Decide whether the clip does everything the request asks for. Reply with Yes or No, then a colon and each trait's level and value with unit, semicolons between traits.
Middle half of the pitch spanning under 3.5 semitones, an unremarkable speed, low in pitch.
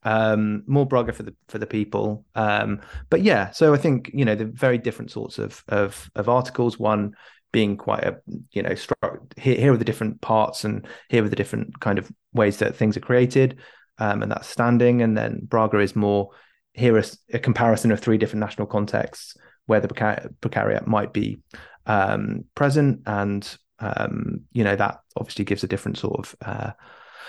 Yes: narrow, 2.6 semitones; average, 190 wpm; low, 110 Hz